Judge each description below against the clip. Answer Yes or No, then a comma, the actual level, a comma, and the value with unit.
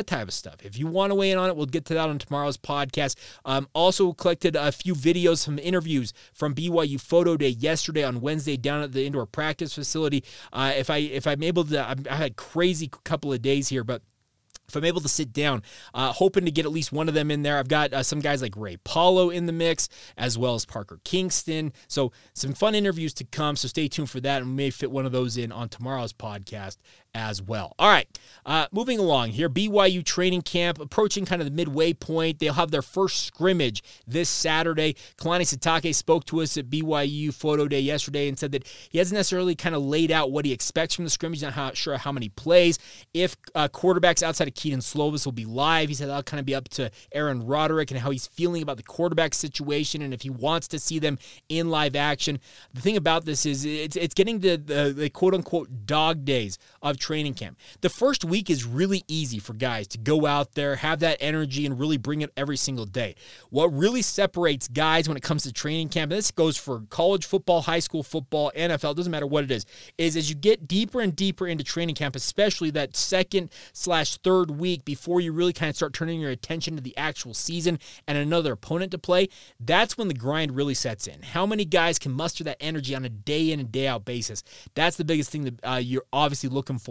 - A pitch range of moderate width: Yes, average, 3.7 semitones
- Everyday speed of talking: No, fast, 230 wpm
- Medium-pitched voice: Yes, medium, 150 Hz